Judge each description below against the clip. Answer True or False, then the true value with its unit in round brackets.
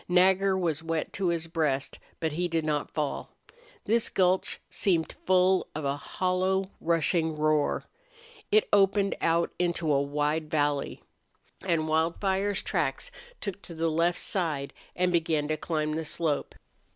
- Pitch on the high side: False (165 Hz)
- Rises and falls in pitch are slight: False (3.2 semitones)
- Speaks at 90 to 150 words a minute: True (145 wpm)